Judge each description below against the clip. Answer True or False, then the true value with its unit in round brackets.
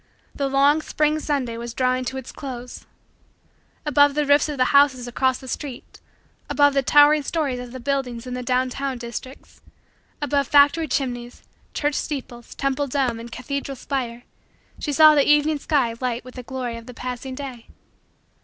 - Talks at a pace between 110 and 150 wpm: False (175 wpm)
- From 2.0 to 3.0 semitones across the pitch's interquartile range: True (2.5 semitones)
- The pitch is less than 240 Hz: False (265 Hz)